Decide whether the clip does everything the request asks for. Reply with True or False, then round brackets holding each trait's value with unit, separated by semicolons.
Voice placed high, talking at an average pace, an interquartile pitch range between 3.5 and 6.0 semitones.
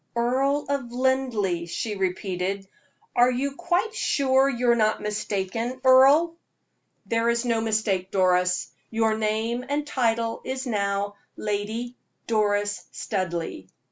False (225 Hz; 120 wpm; 4.2 semitones)